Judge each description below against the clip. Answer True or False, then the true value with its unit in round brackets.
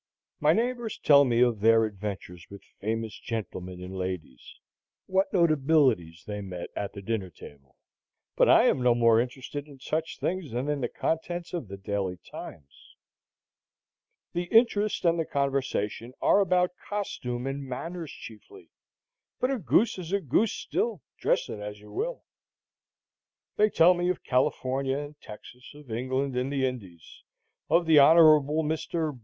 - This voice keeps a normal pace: True (155 wpm)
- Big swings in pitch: True (7.5 semitones)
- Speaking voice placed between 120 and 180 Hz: True (135 Hz)